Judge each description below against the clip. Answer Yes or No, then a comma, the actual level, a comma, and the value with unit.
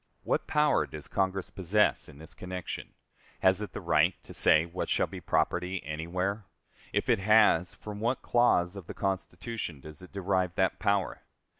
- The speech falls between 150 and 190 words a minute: Yes, average, 170 wpm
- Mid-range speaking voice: No, very low, 95 Hz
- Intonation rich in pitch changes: No, average, 2.8 semitones